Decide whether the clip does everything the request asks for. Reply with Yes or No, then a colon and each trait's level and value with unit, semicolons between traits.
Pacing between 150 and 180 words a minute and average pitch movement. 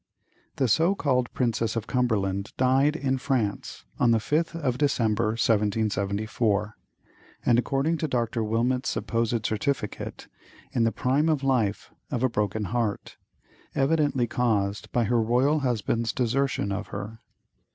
No: slow, 135 wpm; average, 3.7 semitones